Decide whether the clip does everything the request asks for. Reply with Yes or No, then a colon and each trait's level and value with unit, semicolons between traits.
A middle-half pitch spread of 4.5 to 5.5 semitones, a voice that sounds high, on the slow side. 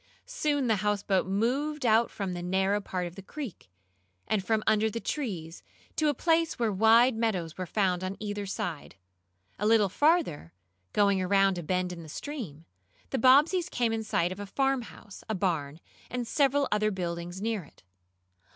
No: average, 4.9 semitones; high, 210 Hz; average, 175 wpm